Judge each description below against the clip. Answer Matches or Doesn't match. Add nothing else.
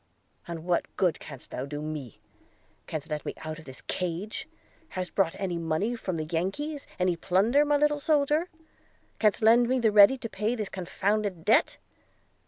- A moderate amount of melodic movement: Doesn't match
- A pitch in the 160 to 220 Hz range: Matches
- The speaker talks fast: Doesn't match